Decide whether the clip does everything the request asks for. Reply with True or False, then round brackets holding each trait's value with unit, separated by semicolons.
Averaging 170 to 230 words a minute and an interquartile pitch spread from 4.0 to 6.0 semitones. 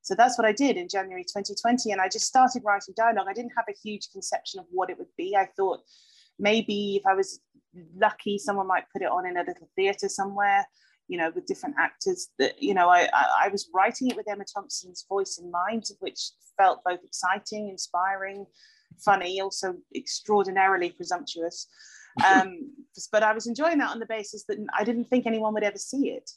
True (200 wpm; 4.3 semitones)